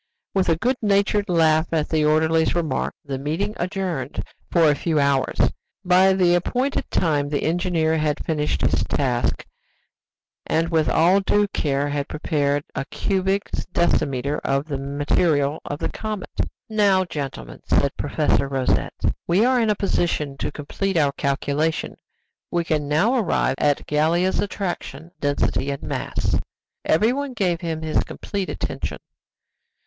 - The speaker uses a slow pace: No, average, 145 wpm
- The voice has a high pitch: No, medium, 160 Hz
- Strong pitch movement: No, average, 4.7 semitones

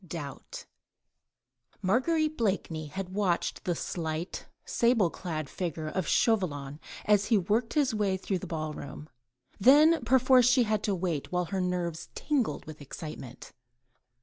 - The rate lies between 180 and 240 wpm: No, average, 145 wpm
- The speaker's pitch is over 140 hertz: Yes, medium, 185 Hz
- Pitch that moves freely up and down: Yes, wide, 6.3 semitones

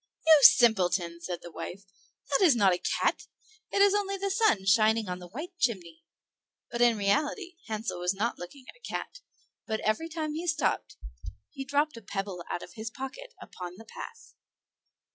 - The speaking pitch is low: No, high, 230 Hz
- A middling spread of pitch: No, wide, 8.4 semitones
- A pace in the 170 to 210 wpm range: Yes, average, 180 wpm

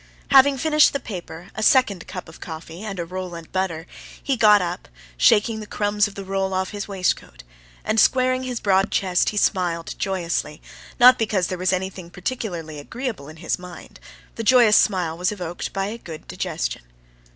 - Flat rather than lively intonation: No, average, 3.9 semitones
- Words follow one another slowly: No, average, 180 wpm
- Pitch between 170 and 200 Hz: Yes, high, 190 Hz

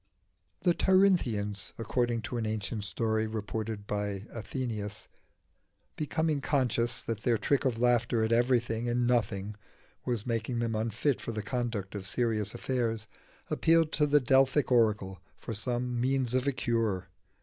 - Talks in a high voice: No, low, 115 Hz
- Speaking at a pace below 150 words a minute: Yes, average, 140 wpm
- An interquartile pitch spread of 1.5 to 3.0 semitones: Yes, average, 2.7 semitones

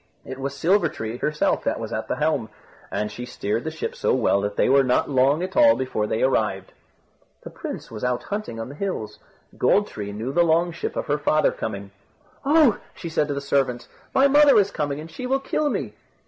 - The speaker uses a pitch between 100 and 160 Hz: Yes, medium, 140 Hz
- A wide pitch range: Yes, wide, 6.9 semitones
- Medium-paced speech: No, fast, 220 wpm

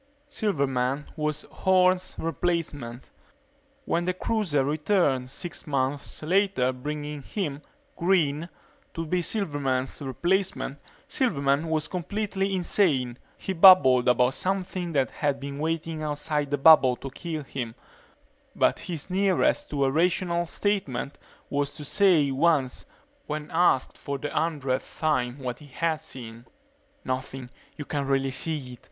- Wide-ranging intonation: No, average, 4.6 semitones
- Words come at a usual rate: No, slow, 130 wpm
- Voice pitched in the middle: Yes, medium, 150 Hz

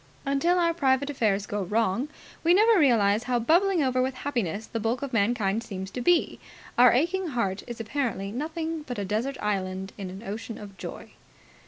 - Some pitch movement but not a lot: No, wide, 5.8 semitones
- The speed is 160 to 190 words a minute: Yes, average, 185 wpm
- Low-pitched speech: No, high, 240 Hz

